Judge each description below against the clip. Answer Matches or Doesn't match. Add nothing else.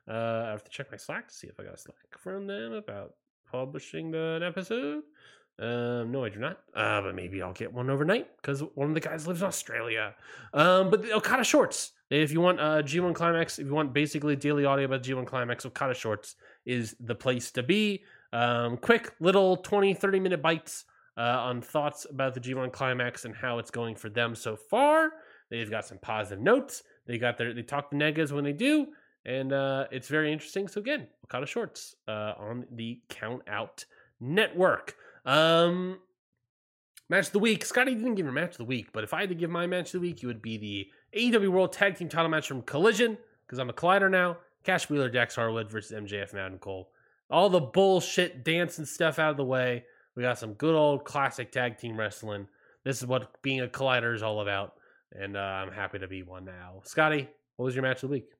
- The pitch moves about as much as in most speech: Doesn't match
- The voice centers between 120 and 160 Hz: Matches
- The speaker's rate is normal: Doesn't match